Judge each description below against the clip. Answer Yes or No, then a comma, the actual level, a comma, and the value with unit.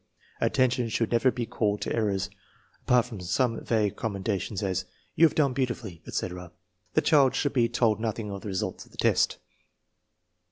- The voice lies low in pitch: Yes, low, 115 Hz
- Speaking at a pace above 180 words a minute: Yes, average, 190 wpm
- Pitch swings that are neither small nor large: Yes, average, 4.0 semitones